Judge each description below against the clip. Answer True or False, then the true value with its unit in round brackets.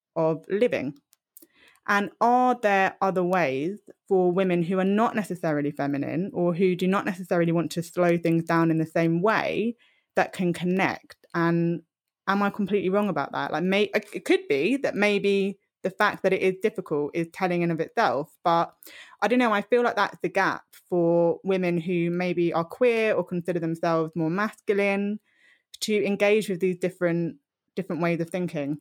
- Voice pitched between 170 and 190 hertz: True (185 Hz)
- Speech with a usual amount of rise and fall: True (3.4 semitones)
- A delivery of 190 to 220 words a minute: False (175 wpm)